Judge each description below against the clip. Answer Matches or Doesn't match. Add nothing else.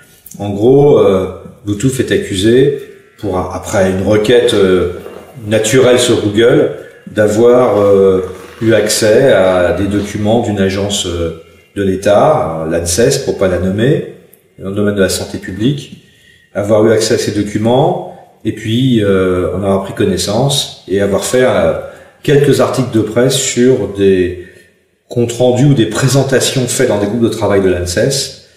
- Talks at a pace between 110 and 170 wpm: Matches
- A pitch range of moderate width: Matches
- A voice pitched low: Matches